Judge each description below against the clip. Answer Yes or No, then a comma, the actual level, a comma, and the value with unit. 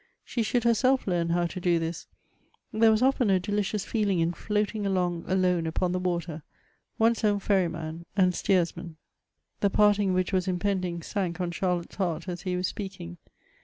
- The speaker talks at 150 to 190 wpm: Yes, average, 170 wpm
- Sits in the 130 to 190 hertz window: Yes, medium, 185 Hz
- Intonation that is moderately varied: Yes, average, 3.0 semitones